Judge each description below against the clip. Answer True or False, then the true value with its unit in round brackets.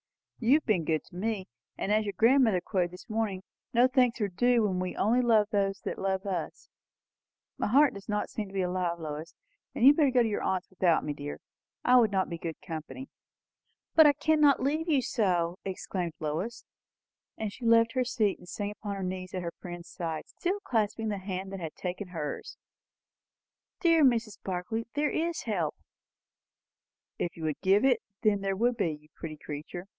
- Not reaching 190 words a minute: False (195 wpm)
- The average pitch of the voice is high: True (200 Hz)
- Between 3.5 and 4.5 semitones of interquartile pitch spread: False (4.9 semitones)